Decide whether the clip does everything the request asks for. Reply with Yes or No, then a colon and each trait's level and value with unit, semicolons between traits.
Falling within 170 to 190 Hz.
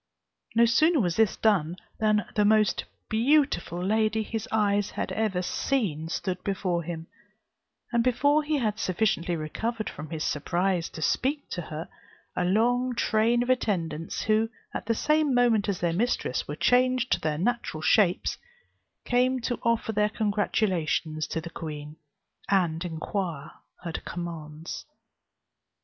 No: high, 205 Hz